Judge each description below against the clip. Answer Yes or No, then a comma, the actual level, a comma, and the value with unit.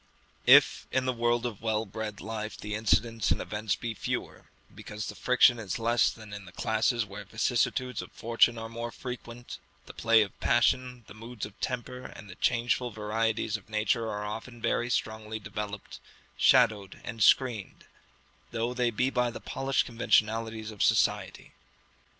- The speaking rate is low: No, average, 165 wpm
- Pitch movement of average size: No, narrow, 2.0 semitones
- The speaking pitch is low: Yes, low, 115 Hz